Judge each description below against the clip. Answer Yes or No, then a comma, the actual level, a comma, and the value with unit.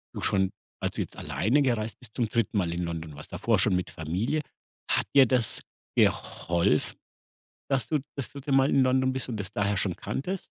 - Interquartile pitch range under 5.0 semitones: No, wide, 6.3 semitones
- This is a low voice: Yes, low, 110 Hz